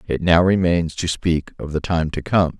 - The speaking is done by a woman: No, male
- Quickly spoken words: Yes, fast, 230 wpm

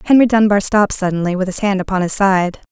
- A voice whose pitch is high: Yes, high, 195 Hz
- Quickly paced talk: Yes, fast, 220 wpm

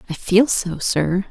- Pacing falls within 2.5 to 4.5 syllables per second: Yes, 3.6 syllables/s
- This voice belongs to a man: No, female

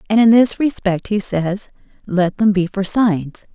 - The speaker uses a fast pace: No, average, 185 wpm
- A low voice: No, high, 200 Hz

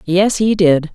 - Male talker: No, female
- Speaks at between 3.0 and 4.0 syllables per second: Yes, 3.5 syllables/s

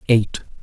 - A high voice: No, low, 110 Hz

